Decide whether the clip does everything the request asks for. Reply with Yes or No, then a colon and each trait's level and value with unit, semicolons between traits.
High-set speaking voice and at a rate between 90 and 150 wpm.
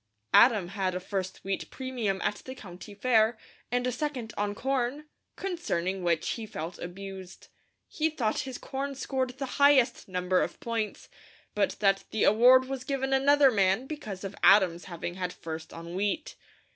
No: high, 215 Hz; average, 165 wpm